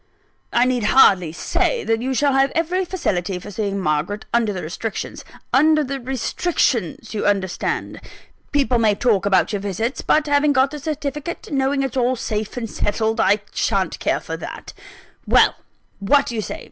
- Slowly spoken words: No, average, 175 wpm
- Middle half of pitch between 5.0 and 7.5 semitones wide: Yes, wide, 5.4 semitones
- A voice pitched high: Yes, high, 240 Hz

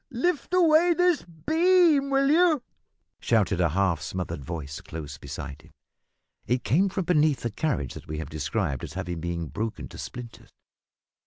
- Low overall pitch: Yes, low, 120 Hz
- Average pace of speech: Yes, average, 160 wpm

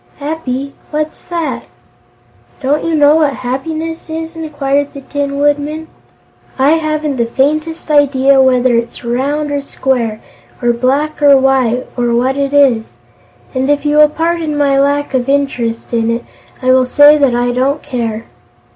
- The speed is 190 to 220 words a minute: No, average, 155 wpm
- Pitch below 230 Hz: No, very high, 280 Hz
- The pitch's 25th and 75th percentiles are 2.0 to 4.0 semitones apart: Yes, average, 2.9 semitones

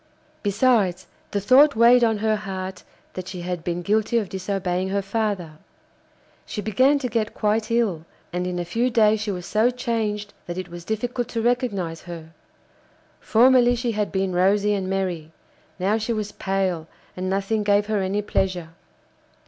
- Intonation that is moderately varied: Yes, average, 3.3 semitones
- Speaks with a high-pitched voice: Yes, high, 205 Hz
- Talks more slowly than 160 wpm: No, average, 170 wpm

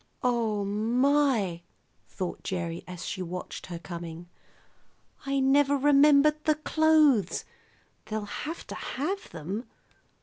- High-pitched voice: Yes, high, 235 Hz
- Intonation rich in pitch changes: Yes, wide, 8.0 semitones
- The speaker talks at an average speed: No, slow, 110 wpm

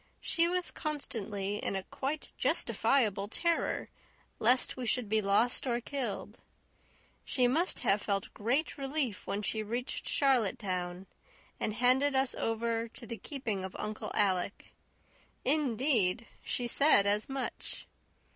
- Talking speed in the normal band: No, slow, 130 wpm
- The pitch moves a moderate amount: Yes, average, 4.8 semitones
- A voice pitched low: No, high, 235 Hz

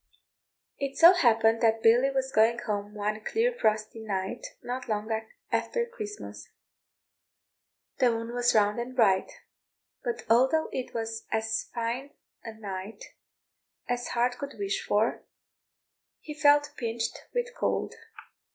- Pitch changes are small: No, average, 3.6 semitones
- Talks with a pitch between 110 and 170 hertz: No, high, 235 Hz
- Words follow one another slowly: Yes, slow, 130 wpm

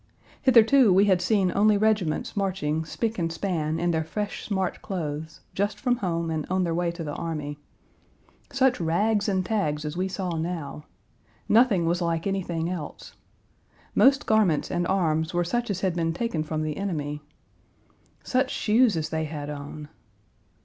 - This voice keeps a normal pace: Yes, average, 165 wpm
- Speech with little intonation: No, average, 4.3 semitones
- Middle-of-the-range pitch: Yes, medium, 175 Hz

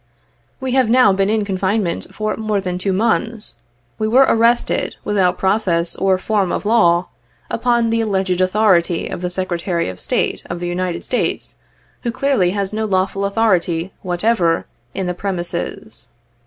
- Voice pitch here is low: No, high, 195 Hz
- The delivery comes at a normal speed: Yes, average, 155 wpm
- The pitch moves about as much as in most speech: Yes, average, 3.6 semitones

